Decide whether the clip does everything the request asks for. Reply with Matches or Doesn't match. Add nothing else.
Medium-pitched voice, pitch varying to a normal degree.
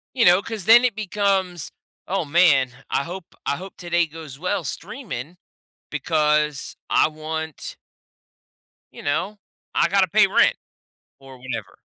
Matches